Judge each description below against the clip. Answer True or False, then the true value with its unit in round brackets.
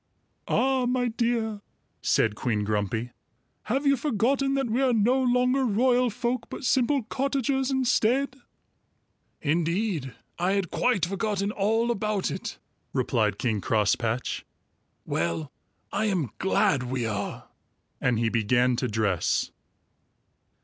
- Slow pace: True (120 wpm)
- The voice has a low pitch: False (210 Hz)